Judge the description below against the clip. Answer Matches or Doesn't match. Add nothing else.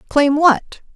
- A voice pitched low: Doesn't match